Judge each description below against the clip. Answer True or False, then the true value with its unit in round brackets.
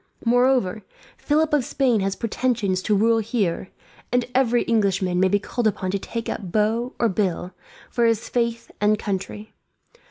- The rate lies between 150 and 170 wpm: True (160 wpm)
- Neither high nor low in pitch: False (220 Hz)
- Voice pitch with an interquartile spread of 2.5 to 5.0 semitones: True (3.5 semitones)